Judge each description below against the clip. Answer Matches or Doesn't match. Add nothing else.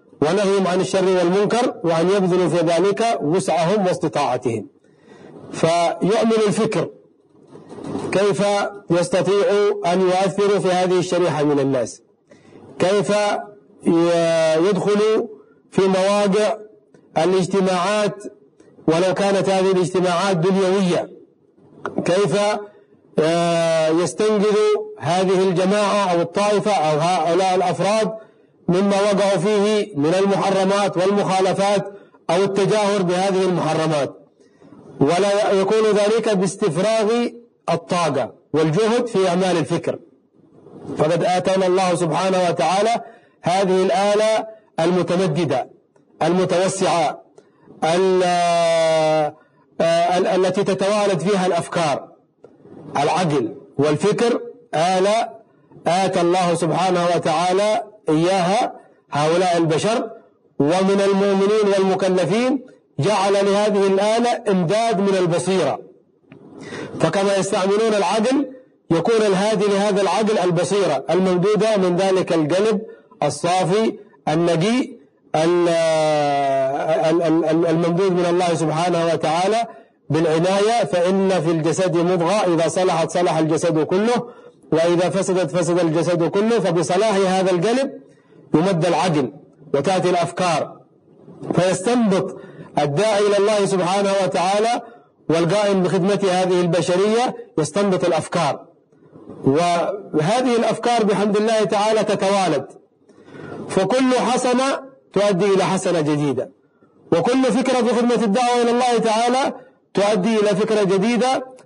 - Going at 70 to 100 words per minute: Matches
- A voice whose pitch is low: Doesn't match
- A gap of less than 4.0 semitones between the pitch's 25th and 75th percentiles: Matches